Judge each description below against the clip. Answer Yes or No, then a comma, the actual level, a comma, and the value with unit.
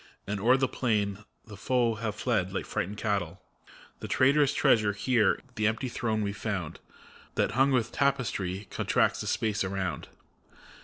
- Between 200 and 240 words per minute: No, average, 155 wpm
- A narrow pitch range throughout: No, average, 3.7 semitones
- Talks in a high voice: No, low, 110 Hz